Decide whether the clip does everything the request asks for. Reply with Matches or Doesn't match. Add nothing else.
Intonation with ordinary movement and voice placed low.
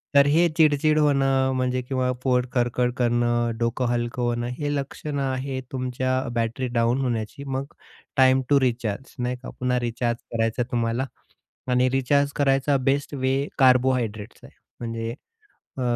Doesn't match